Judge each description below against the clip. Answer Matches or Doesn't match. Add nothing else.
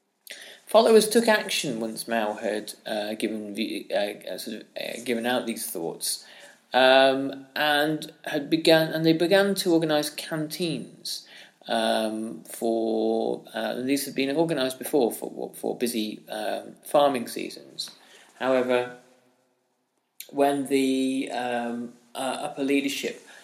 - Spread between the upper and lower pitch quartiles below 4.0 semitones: Doesn't match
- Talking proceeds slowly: Matches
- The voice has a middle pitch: Doesn't match